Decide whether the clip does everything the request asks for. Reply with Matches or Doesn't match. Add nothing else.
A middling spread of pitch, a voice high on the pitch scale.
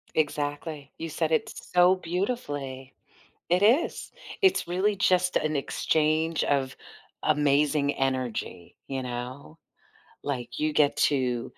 Doesn't match